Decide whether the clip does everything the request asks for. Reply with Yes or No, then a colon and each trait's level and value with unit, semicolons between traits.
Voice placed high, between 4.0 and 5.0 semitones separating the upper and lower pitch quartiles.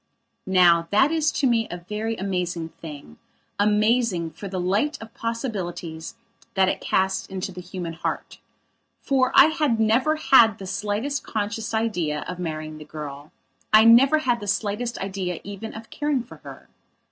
Yes: high, 205 Hz; average, 4.5 semitones